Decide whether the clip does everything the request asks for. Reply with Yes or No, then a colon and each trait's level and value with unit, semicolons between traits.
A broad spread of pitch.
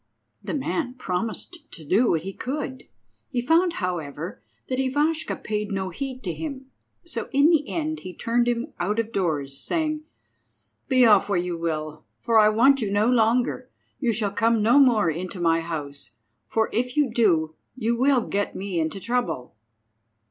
Yes: wide, 6.4 semitones